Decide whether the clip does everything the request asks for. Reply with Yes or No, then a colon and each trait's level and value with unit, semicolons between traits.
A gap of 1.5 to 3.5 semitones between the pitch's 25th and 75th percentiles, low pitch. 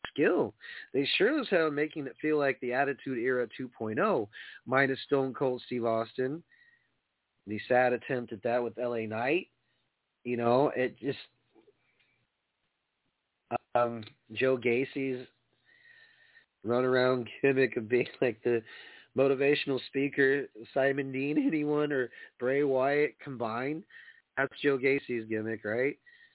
Yes: average, 2.7 semitones; low, 130 Hz